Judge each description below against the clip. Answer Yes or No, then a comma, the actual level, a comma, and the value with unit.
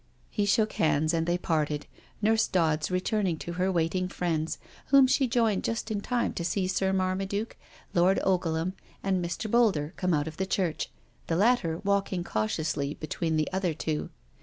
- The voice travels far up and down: No, average, 3.8 semitones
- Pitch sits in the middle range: Yes, medium, 180 Hz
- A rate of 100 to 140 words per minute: No, average, 170 wpm